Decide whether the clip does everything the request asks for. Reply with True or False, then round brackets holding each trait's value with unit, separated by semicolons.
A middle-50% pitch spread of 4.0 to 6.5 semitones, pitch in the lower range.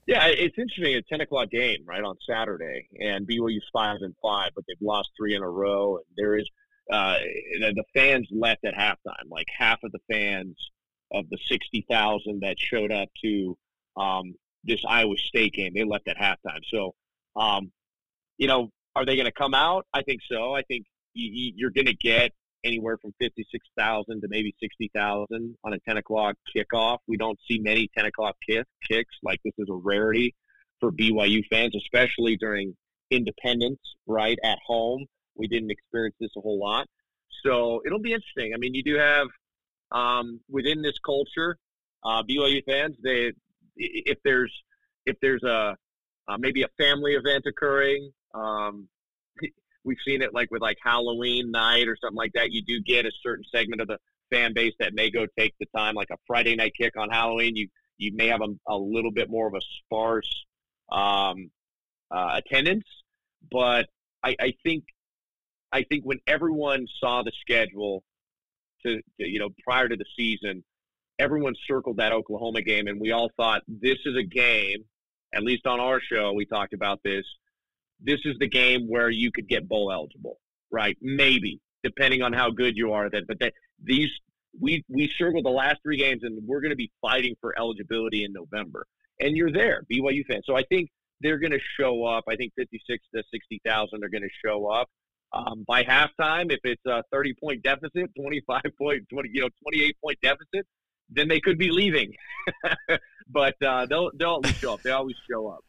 True (4.3 semitones; 120 Hz)